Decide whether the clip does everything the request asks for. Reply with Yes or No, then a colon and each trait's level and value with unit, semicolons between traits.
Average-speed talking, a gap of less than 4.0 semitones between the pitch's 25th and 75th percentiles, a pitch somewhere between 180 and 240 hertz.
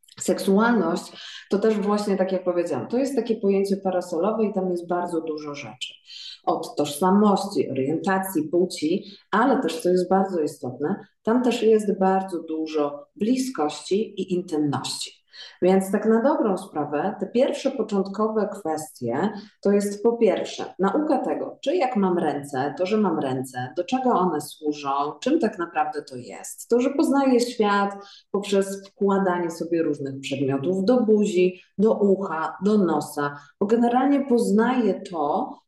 No: average, 145 wpm; average, 5.3 semitones; high, 190 Hz